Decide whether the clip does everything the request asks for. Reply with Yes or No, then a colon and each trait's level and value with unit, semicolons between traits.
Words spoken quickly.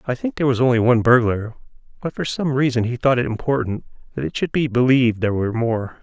Yes: fast, 230 wpm